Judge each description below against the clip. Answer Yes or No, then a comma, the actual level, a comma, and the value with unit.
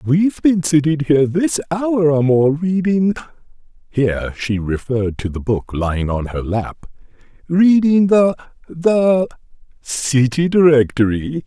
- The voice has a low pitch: No, medium, 150 Hz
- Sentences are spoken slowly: Yes, slow, 120 wpm